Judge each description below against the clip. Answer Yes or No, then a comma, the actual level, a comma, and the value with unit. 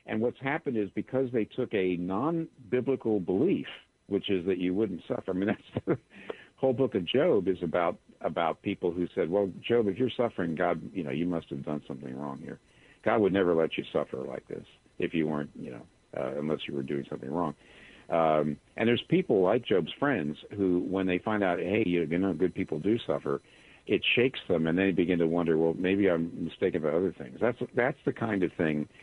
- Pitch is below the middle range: Yes, very low, 95 Hz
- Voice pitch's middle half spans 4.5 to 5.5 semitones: Yes, average, 5.0 semitones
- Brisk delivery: Yes, fast, 215 wpm